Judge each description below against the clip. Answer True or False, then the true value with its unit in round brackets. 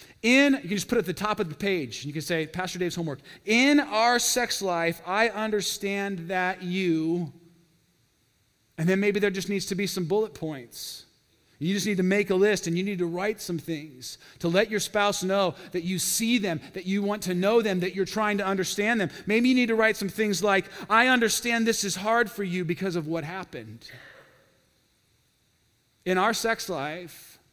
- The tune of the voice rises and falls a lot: False (3.4 semitones)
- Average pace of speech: False (210 wpm)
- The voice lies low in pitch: False (195 Hz)